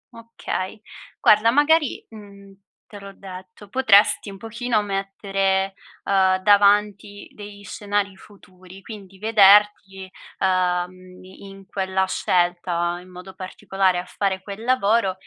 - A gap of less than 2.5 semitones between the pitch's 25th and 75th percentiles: Yes, narrow, 1.8 semitones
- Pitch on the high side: Yes, high, 195 Hz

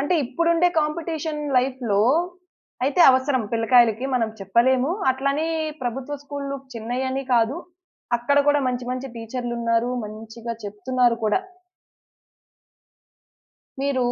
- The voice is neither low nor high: No, very high, 255 Hz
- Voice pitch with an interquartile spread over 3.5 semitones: No, average, 3.2 semitones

